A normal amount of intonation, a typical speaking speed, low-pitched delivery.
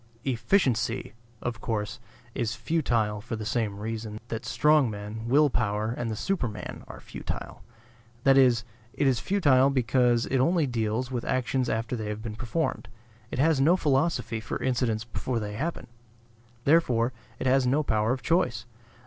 Yes: average, 3.5 semitones; average, 160 wpm; low, 120 Hz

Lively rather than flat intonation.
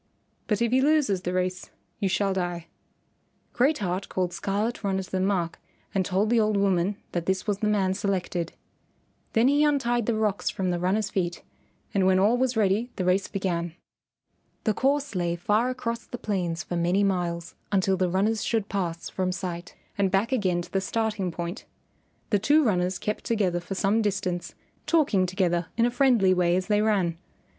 No: average, 3.3 semitones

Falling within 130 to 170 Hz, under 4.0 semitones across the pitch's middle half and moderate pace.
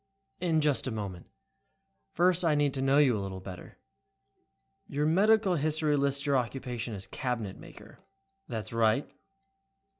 No: low, 135 Hz; wide, 5.5 semitones; average, 145 wpm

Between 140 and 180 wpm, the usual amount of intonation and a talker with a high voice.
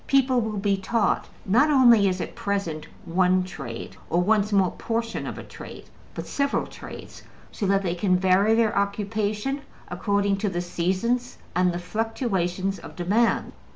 Yes: average, 160 wpm; average, 3.5 semitones; high, 200 Hz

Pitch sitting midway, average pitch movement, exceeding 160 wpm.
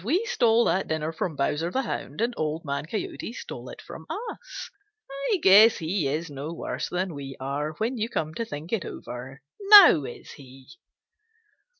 No: medium, 165 Hz; wide, 7.9 semitones; average, 180 wpm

